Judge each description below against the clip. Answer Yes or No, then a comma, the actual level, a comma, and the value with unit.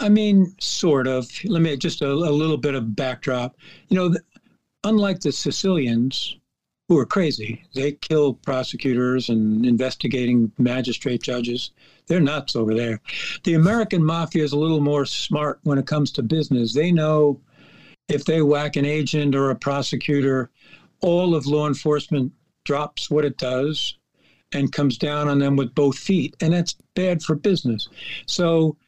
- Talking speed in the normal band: Yes, average, 160 wpm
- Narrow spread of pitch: No, average, 3.7 semitones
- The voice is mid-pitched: Yes, medium, 145 Hz